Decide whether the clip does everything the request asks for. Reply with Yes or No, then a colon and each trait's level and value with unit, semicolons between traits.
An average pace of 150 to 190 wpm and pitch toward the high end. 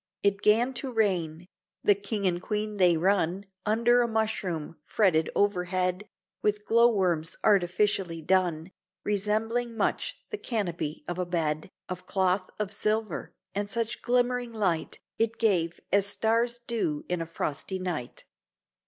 No: average, 140 wpm; high, 200 Hz